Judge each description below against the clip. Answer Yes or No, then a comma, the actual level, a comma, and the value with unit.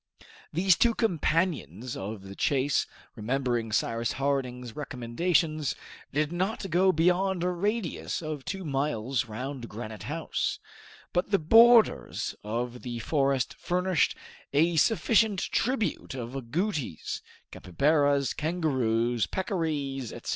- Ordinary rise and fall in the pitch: No, wide, 6.6 semitones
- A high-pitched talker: No, medium, 145 Hz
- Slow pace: Yes, slow, 110 wpm